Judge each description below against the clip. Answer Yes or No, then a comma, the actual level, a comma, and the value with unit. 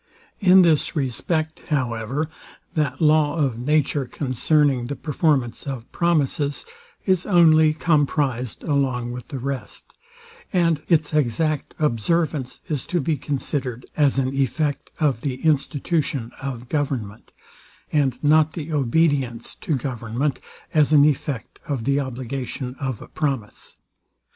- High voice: No, medium, 140 Hz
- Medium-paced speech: No, slow, 125 wpm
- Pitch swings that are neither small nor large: Yes, average, 3.3 semitones